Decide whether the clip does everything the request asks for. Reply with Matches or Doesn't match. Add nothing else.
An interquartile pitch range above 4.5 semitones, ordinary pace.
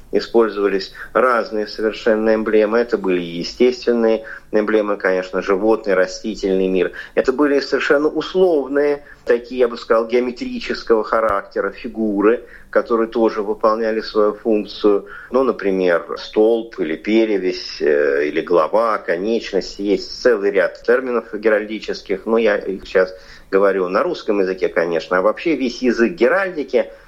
Matches